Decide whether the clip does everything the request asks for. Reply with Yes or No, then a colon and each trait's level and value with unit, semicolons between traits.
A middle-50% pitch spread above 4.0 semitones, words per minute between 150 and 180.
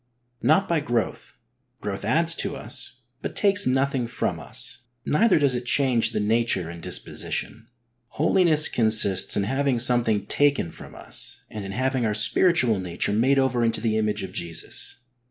Yes: average, 4.8 semitones; average, 160 wpm